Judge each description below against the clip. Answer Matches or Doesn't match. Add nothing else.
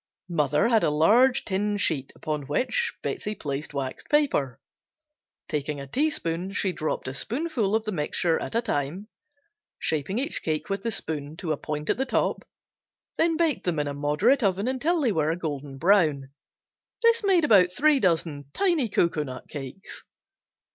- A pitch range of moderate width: Doesn't match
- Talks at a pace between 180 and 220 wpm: Doesn't match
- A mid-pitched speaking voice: Matches